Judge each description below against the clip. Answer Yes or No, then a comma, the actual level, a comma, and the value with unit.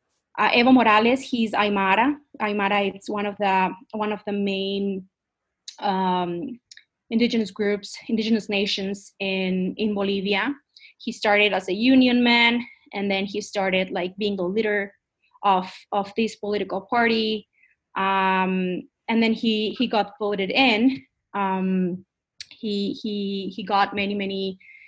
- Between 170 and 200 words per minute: No, slow, 135 wpm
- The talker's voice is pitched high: Yes, high, 205 Hz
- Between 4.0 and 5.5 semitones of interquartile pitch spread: No, average, 2.7 semitones